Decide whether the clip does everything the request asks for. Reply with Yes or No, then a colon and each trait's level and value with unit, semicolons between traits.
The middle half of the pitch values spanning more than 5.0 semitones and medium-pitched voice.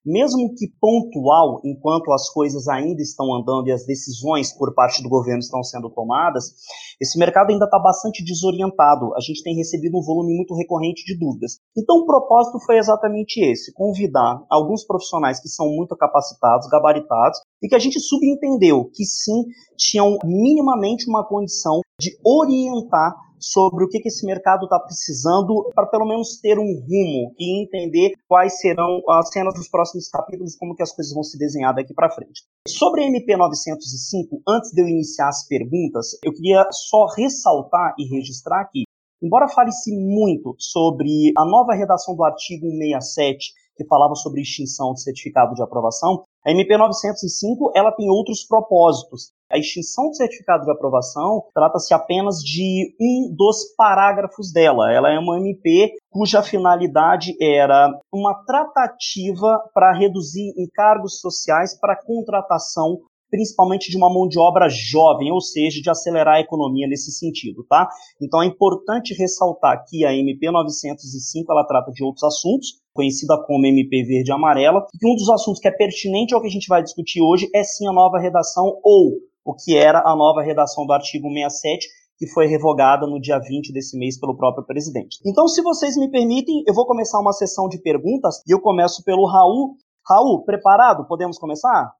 Yes: wide, 5.6 semitones; medium, 180 Hz